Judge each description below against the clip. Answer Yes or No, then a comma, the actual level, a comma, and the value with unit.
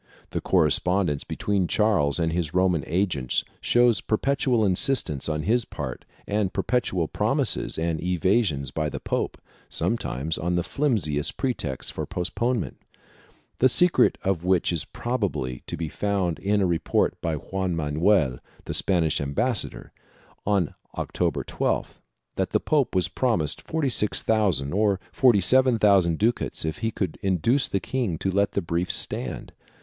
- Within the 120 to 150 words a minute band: Yes, average, 145 wpm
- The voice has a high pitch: No, very low, 95 Hz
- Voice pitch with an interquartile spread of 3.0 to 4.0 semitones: No, average, 5.3 semitones